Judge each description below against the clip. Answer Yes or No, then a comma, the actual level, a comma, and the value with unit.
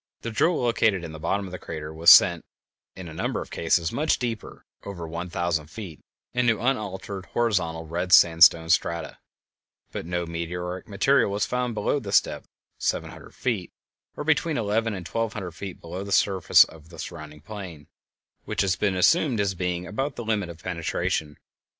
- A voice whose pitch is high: No, very low, 95 Hz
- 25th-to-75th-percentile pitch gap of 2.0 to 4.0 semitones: No, average, 4.6 semitones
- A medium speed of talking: Yes, average, 180 wpm